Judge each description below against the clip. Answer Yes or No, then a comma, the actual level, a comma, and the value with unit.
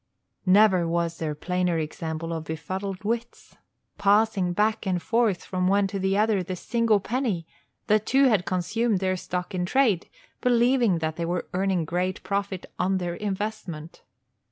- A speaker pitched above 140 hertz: Yes, high, 190 Hz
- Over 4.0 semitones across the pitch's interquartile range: No, average, 3.4 semitones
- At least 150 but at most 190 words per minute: Yes, average, 155 wpm